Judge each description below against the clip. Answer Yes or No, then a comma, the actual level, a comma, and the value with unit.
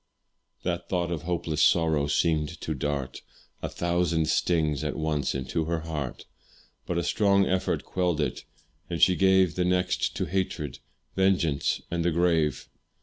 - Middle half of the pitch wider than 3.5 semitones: No, average, 2.7 semitones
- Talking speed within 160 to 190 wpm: No, average, 150 wpm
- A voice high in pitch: No, very low, 85 Hz